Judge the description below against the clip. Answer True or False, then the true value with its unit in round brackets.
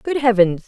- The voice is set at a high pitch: True (225 Hz)